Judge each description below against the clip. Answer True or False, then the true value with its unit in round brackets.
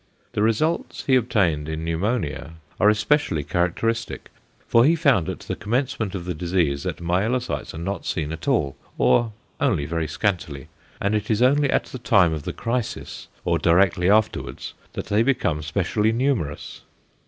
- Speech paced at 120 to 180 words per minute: True (165 wpm)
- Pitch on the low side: True (100 Hz)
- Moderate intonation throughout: False (6.0 semitones)